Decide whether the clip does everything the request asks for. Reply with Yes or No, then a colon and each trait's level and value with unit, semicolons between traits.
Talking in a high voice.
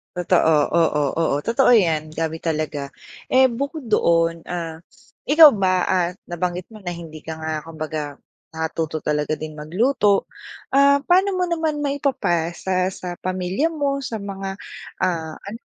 No: medium, 180 Hz